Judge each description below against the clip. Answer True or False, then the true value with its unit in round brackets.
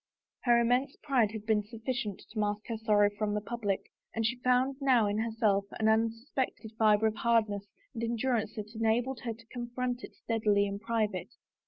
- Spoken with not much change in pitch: True (2.3 semitones)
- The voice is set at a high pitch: True (225 Hz)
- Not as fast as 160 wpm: False (180 wpm)